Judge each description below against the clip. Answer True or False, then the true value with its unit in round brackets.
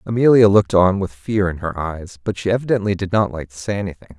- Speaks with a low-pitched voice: True (100 Hz)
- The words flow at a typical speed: False (245 wpm)